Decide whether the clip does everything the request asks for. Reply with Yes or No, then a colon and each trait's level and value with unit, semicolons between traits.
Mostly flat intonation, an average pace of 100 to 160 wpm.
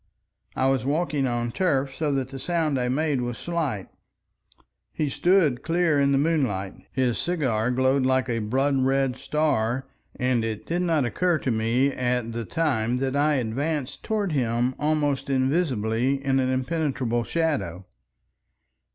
No: average, 3.7 semitones; average, 150 wpm